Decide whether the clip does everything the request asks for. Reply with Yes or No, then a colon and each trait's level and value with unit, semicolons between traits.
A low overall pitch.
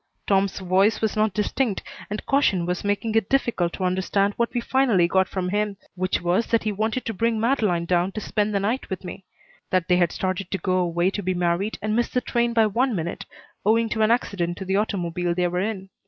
No: high, 200 Hz